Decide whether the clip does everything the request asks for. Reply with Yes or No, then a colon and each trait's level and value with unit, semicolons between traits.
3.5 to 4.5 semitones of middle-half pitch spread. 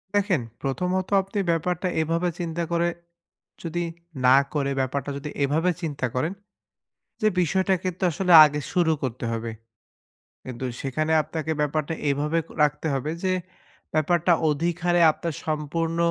No: average, 3.1 semitones